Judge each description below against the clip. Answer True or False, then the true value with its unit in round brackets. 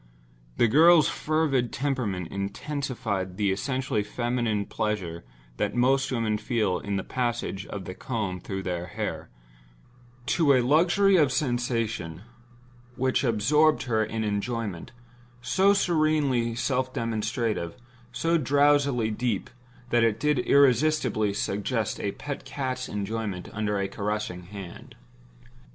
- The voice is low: True (115 Hz)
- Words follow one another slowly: True (120 wpm)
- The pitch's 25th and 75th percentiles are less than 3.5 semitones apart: False (4.8 semitones)